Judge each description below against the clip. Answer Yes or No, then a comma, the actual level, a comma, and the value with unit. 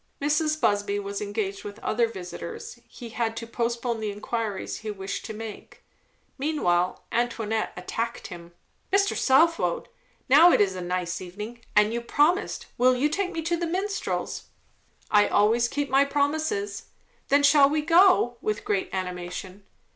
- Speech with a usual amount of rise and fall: No, wide, 6.2 semitones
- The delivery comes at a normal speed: Yes, average, 155 wpm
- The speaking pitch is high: Yes, high, 230 Hz